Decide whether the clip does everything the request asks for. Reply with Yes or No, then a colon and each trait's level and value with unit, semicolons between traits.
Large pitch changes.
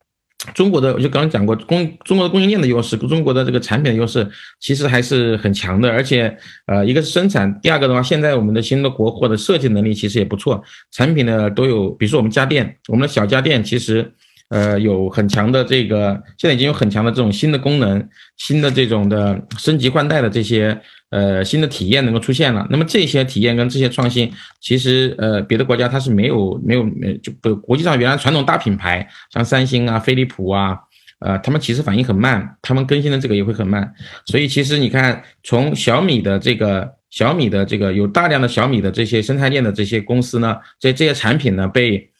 No: average, 4.3 semitones